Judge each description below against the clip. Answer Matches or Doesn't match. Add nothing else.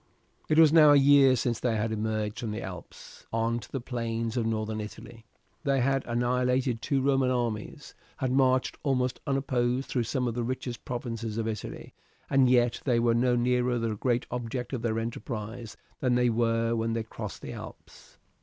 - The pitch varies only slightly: Matches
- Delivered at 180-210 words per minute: Matches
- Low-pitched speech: Matches